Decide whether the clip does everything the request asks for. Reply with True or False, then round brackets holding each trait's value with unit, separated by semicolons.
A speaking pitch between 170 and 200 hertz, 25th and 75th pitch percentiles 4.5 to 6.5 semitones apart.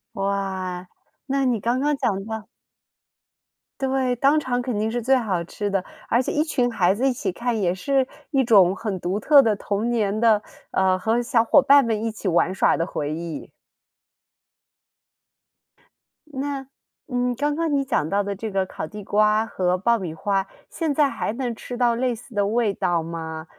False (220 Hz; 4.8 semitones)